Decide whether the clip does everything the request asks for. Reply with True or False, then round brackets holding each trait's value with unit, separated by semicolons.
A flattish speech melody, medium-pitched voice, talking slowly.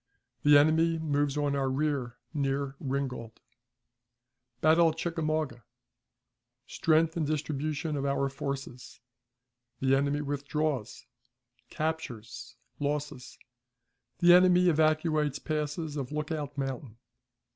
True (2.3 semitones; 145 Hz; 100 wpm)